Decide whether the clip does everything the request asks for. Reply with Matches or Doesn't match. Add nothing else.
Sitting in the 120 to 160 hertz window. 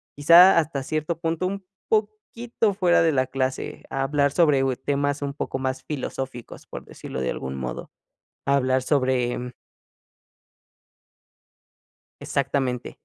Matches